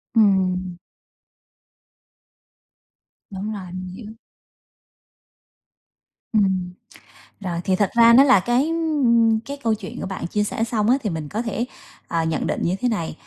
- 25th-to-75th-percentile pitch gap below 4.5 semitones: Yes, average, 4.0 semitones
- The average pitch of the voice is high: Yes, high, 210 Hz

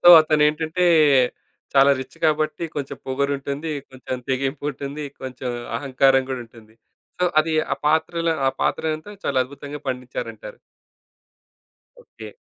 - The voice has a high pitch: No, medium, 140 Hz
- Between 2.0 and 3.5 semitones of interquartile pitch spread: Yes, average, 2.9 semitones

